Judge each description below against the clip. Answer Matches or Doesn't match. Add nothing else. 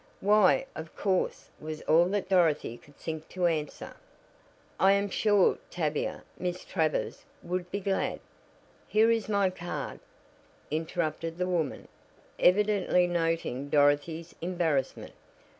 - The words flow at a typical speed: Doesn't match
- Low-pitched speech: Doesn't match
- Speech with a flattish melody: Doesn't match